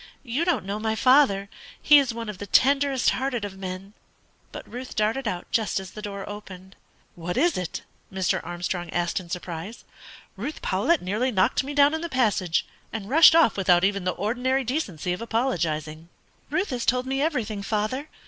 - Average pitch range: No, wide, 5.9 semitones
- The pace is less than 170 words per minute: No, average, 185 wpm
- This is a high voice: Yes, high, 215 Hz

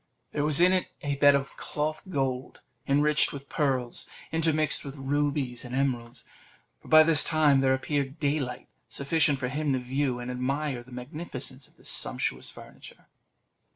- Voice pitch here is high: No, medium, 140 Hz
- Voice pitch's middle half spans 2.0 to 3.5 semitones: Yes, narrow, 2.6 semitones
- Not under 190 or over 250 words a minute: No, average, 165 wpm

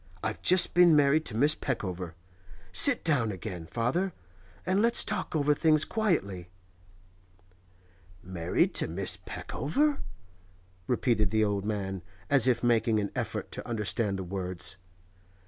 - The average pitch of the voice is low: Yes, low, 115 Hz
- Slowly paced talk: Yes, slow, 130 wpm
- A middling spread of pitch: No, wide, 8.2 semitones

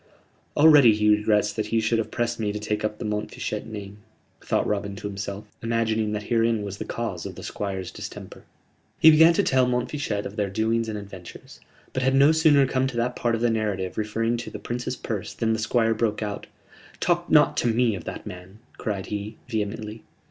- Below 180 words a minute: No, fast, 205 wpm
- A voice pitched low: Yes, low, 110 Hz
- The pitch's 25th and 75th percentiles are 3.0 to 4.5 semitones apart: No, narrow, 2.4 semitones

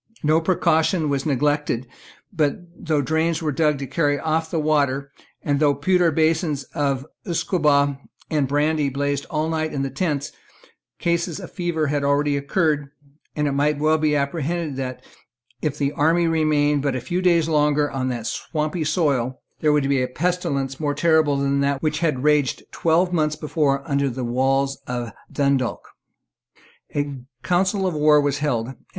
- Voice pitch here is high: No, medium, 150 Hz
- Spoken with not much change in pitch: Yes, narrow, 2.3 semitones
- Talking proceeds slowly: No, average, 165 wpm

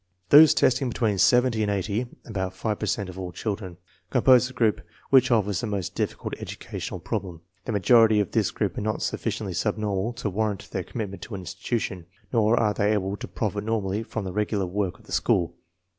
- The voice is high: No, low, 105 Hz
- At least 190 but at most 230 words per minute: Yes, average, 200 wpm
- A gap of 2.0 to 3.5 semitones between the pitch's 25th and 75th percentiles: Yes, average, 2.8 semitones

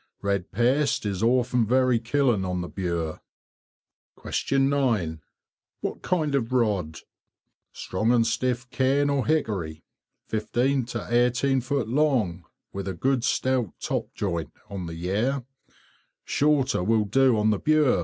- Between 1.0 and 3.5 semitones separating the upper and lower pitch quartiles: No, average, 5.3 semitones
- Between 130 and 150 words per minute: Yes, slow, 135 wpm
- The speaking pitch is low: Yes, low, 120 Hz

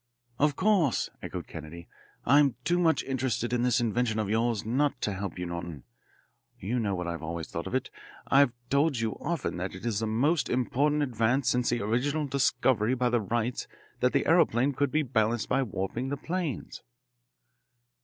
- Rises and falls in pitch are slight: No, average, 4.5 semitones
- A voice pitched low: Yes, low, 120 Hz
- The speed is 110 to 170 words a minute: No, average, 180 wpm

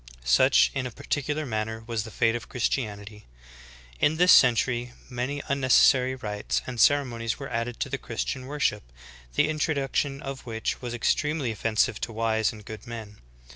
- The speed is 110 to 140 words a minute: No, average, 165 wpm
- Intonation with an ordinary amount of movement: Yes, average, 3.5 semitones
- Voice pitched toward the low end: Yes, low, 120 Hz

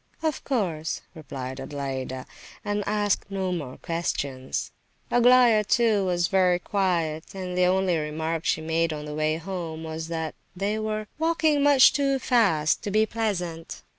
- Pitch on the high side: No, medium, 180 Hz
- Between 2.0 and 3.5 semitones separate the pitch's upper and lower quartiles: No, average, 5.1 semitones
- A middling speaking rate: Yes, average, 155 wpm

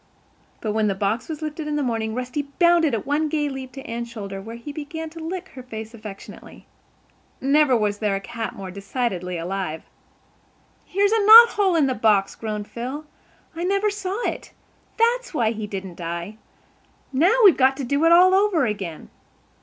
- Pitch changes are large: Yes, wide, 7.4 semitones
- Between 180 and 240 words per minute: Yes, average, 185 wpm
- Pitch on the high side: Yes, very high, 255 Hz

